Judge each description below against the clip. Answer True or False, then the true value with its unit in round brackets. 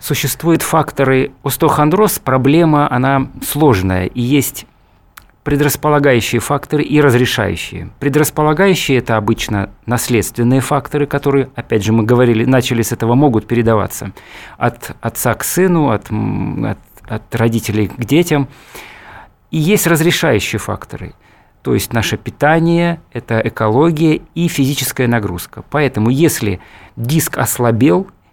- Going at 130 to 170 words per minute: False (115 wpm)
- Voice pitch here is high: False (130 Hz)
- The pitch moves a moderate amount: True (4.8 semitones)